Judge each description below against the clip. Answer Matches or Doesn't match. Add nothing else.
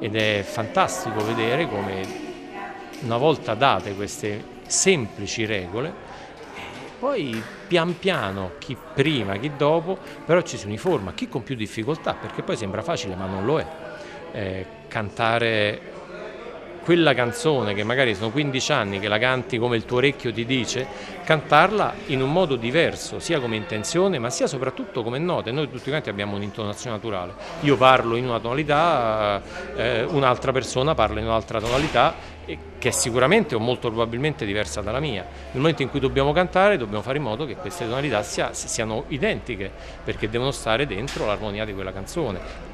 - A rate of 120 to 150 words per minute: Doesn't match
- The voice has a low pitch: Matches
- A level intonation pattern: Doesn't match